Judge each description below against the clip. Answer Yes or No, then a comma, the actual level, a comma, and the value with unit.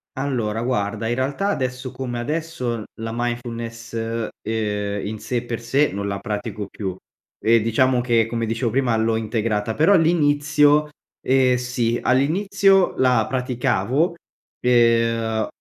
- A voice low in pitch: Yes, low, 120 Hz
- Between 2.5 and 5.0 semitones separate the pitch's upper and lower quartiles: Yes, average, 2.9 semitones